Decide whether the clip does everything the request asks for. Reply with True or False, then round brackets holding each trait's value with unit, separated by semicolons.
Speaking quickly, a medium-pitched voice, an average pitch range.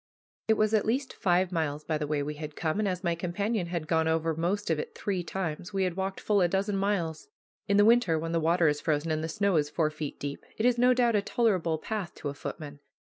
True (260 wpm; 175 Hz; 4.3 semitones)